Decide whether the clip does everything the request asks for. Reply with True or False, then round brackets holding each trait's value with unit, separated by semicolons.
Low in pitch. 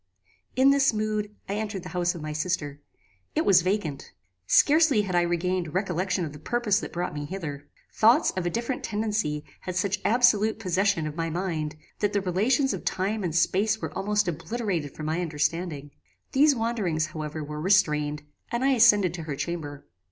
False (185 Hz)